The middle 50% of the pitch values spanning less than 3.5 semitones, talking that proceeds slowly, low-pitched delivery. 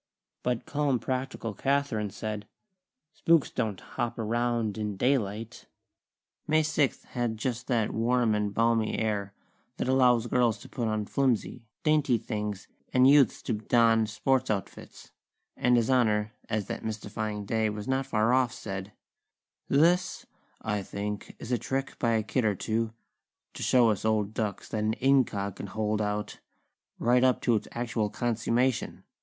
No: average, 2.9 semitones; average, 155 wpm; low, 115 Hz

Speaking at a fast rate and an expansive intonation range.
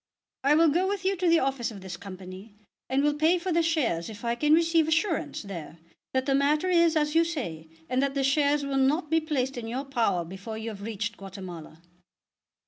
Yes: fast, 220 wpm; wide, 7.4 semitones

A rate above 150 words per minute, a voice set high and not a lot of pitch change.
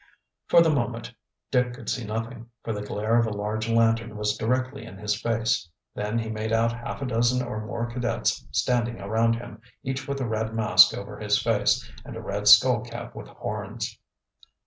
No: average, 190 wpm; low, 115 Hz; narrow, 1.8 semitones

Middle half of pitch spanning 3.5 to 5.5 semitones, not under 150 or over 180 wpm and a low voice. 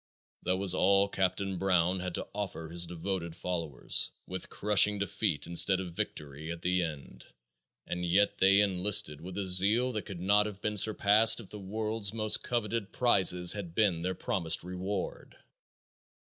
No: average, 2.7 semitones; average, 165 wpm; very low, 95 Hz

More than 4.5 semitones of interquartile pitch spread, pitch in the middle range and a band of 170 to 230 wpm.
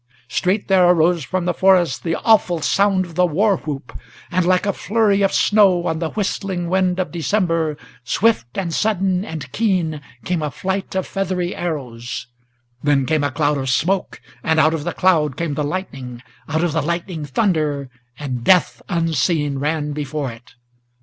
No: average, 4.0 semitones; medium, 170 Hz; average, 175 wpm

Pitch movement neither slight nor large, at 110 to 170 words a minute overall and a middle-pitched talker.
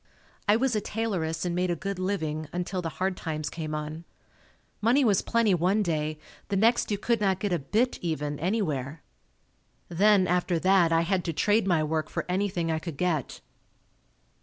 No: average, 4.2 semitones; average, 185 wpm; medium, 180 Hz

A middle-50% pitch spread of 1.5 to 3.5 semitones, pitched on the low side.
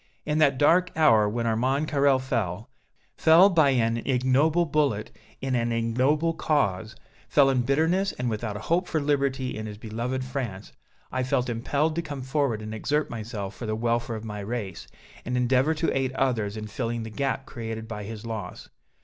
No: average, 4.2 semitones; low, 125 Hz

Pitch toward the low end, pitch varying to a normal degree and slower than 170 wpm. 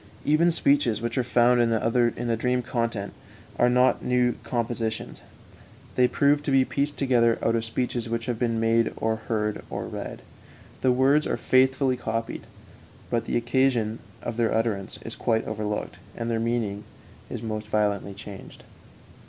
No: low, 115 Hz; narrow, 2.0 semitones; average, 160 wpm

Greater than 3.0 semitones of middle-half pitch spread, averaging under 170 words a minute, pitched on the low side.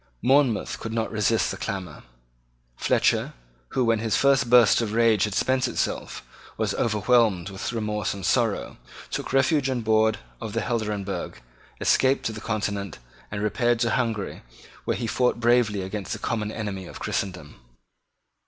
No: average, 2.7 semitones; average, 155 wpm; low, 110 Hz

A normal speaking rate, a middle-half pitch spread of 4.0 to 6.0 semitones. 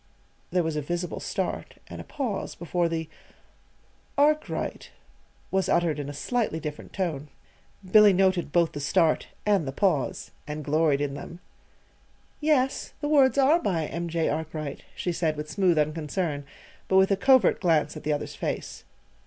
Yes: average, 160 wpm; average, 4.3 semitones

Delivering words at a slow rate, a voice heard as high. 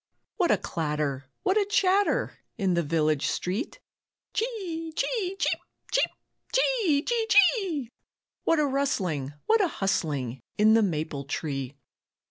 Yes: slow, 130 wpm; very high, 255 Hz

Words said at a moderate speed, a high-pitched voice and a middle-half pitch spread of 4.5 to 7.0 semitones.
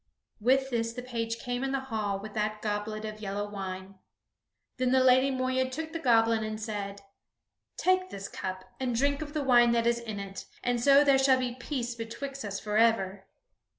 No: average, 190 wpm; high, 235 Hz; average, 3.7 semitones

